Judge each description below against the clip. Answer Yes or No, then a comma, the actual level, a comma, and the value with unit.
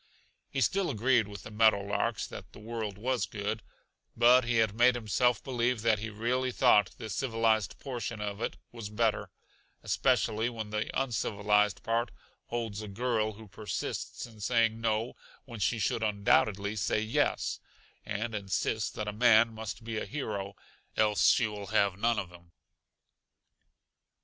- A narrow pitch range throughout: Yes, narrow, 2.2 semitones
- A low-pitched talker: Yes, low, 110 Hz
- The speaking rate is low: No, average, 160 wpm